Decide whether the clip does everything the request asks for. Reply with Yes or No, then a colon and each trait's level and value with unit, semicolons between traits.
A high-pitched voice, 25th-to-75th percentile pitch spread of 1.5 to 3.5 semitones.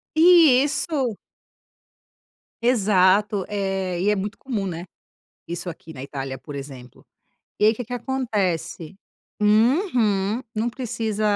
No: high, 210 Hz; average, 5.0 semitones